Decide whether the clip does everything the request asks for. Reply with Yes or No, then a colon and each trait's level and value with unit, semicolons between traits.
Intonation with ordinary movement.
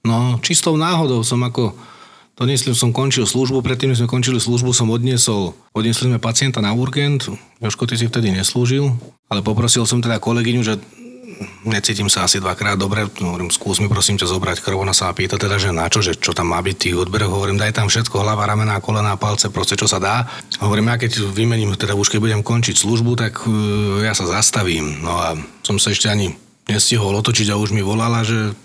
Yes: average, 3.2 semitones